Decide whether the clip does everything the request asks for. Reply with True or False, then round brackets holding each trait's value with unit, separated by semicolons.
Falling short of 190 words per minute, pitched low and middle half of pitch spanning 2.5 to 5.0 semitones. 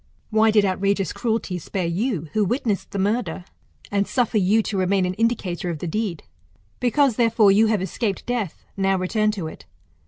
False (180 wpm; 200 Hz; 3.2 semitones)